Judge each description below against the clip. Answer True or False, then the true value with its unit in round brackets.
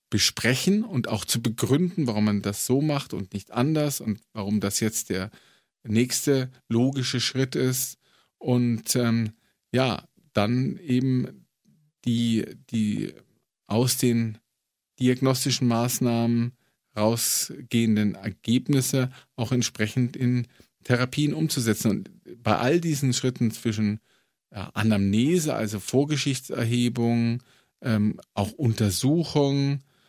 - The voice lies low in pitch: True (120 Hz)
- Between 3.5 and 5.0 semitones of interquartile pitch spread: False (3.0 semitones)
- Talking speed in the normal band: False (105 wpm)